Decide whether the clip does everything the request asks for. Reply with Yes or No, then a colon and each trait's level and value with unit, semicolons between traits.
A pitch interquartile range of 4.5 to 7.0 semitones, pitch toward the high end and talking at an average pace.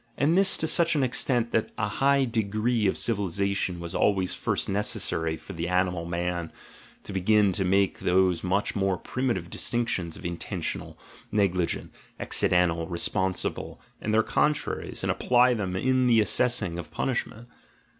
No: average, 4.9 semitones; low, 100 Hz; average, 160 wpm